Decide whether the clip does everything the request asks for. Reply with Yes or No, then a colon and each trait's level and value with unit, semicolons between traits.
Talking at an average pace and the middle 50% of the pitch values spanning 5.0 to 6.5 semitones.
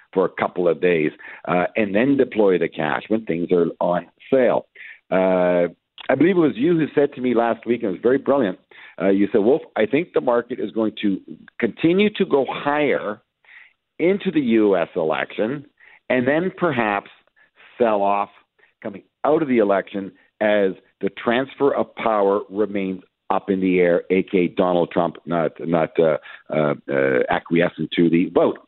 Yes: average, 175 wpm; wide, 5.4 semitones